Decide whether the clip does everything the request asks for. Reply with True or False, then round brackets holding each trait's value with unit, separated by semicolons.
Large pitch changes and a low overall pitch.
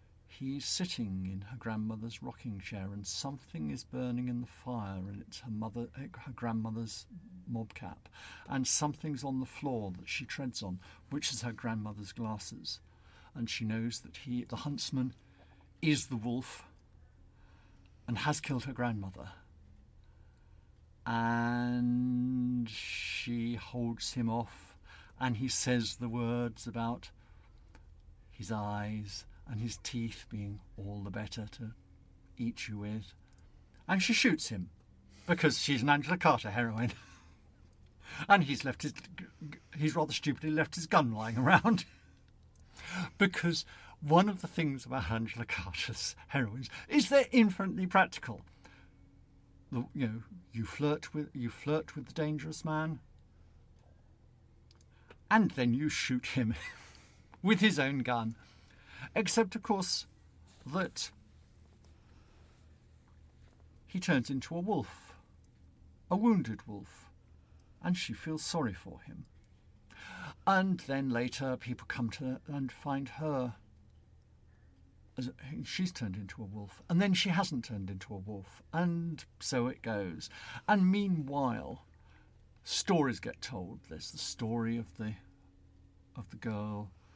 True (6.1 semitones; 115 Hz)